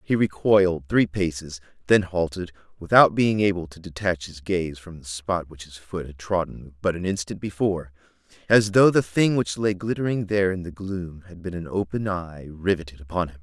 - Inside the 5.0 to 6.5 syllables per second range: Yes, 5.1 syllables/s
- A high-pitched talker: No, very low, 90 Hz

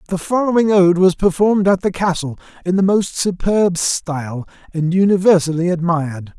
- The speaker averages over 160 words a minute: No, average, 150 wpm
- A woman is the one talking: No, male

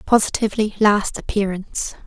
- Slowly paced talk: Yes, slow, 85 wpm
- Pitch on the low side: No, high, 205 Hz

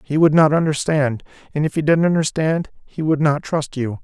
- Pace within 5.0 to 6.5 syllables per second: Yes, 5.2 syllables/s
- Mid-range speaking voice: Yes, medium, 150 Hz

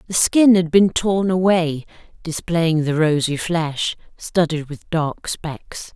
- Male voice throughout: No, female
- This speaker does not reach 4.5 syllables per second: Yes, 3.5 syllables/s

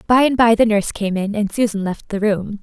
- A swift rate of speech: Yes, fast, 275 wpm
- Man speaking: No, female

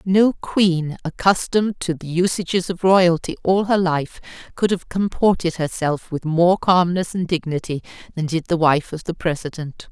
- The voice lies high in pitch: No, medium, 175 Hz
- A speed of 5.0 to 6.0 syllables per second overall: No, 4.6 syllables/s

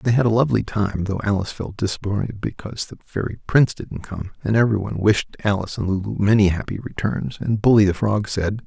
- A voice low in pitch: Yes, low, 105 Hz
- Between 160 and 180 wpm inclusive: No, average, 200 wpm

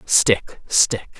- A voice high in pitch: No, low, 115 Hz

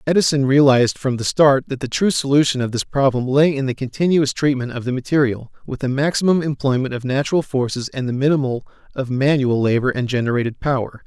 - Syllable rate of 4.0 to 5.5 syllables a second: No, 6.1 syllables/s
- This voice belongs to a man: Yes, male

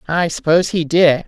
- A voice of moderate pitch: Yes, medium, 165 Hz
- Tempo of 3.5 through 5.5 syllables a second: Yes, 5.4 syllables/s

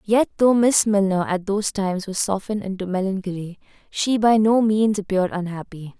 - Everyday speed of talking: Yes, average, 170 wpm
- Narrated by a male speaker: No, female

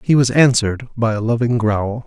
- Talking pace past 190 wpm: Yes, fast, 205 wpm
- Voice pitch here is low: Yes, low, 115 Hz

